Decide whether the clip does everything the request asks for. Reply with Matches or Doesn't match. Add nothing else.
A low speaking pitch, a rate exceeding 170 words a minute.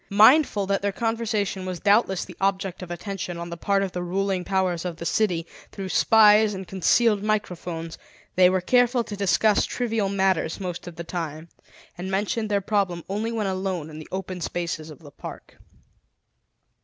Doesn't match